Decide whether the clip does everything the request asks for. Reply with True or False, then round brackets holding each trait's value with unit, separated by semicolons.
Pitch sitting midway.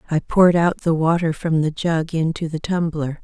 True (165 Hz)